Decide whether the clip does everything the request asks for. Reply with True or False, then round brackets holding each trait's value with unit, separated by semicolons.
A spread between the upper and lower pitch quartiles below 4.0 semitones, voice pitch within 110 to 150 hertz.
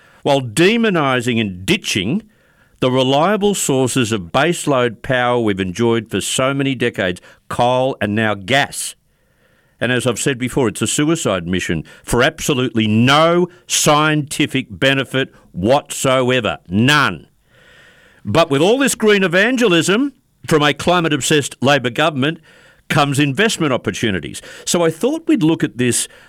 False (5.0 semitones; 135 Hz)